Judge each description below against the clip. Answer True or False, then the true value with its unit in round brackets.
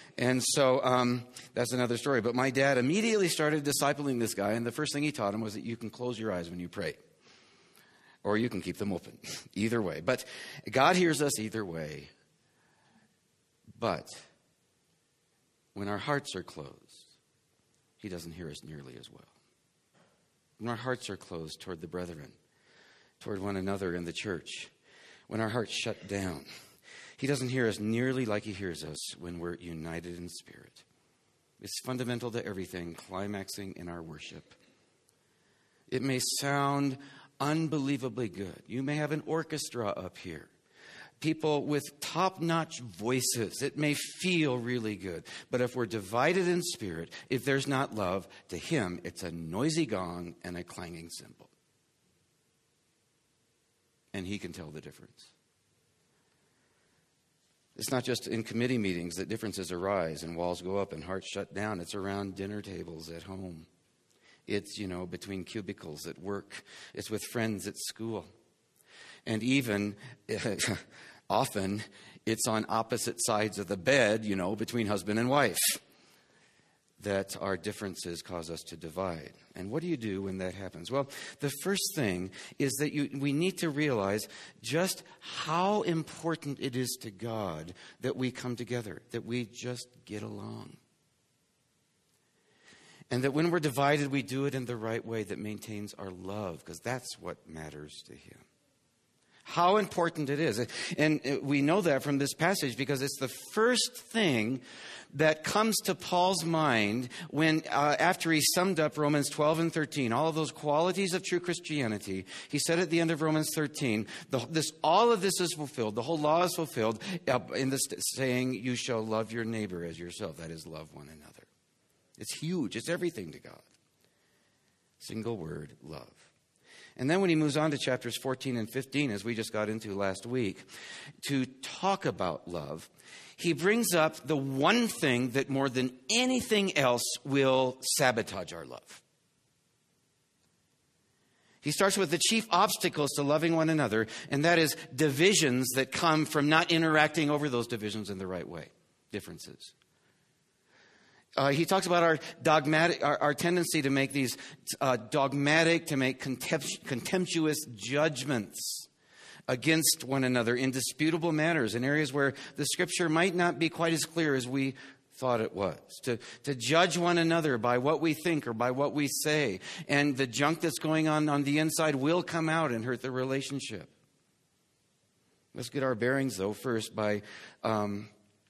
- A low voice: True (130 Hz)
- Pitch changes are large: True (6.8 semitones)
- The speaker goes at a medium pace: True (165 wpm)